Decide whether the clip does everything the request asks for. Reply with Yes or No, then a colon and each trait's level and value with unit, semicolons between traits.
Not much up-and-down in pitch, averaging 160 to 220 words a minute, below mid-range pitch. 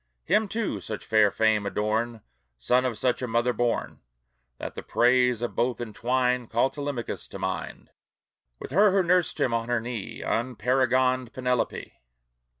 No: narrow, 2.2 semitones; average, 150 wpm; low, 125 Hz